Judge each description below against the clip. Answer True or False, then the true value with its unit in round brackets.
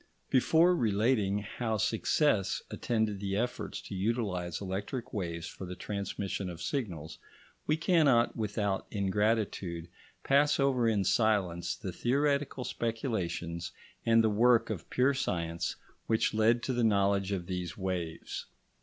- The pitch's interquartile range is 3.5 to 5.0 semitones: True (4.4 semitones)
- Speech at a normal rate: False (130 wpm)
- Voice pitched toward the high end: False (105 Hz)